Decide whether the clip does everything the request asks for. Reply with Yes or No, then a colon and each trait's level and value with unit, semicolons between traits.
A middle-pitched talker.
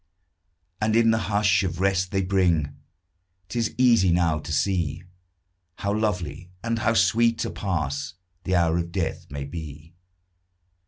No: very low, 95 Hz